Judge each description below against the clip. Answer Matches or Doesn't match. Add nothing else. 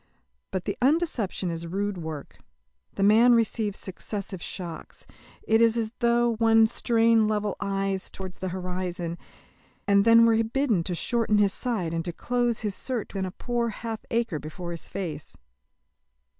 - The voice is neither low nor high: Doesn't match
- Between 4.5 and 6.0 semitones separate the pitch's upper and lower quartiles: Doesn't match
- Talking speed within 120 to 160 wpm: Matches